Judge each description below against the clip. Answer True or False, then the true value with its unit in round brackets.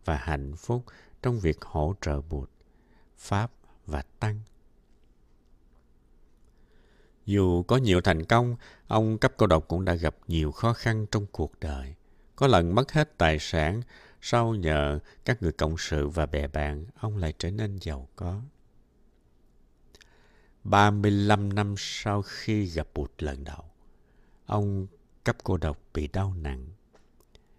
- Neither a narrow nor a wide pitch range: False (6.1 semitones)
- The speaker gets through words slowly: True (140 wpm)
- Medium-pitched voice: False (85 Hz)